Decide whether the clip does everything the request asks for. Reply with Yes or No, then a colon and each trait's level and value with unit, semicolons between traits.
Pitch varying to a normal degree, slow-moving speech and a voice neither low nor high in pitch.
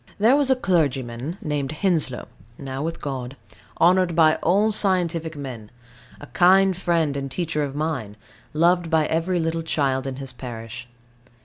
No: average, 4.6 semitones; average, 150 wpm; medium, 155 Hz